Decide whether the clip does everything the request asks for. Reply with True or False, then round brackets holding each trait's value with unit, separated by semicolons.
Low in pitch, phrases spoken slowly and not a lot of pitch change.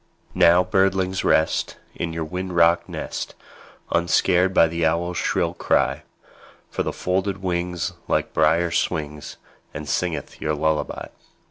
True (85 Hz; 130 wpm; 2.1 semitones)